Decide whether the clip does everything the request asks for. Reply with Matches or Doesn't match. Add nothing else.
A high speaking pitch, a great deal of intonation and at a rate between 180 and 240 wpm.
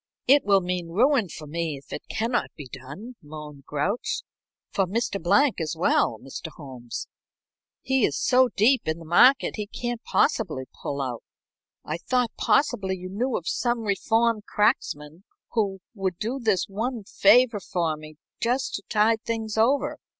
Doesn't match